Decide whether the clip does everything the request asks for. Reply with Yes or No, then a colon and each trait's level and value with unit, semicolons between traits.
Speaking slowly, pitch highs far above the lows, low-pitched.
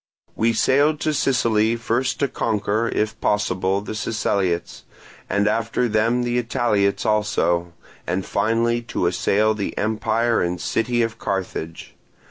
No: slow, 130 wpm; average, 2.8 semitones; low, 110 Hz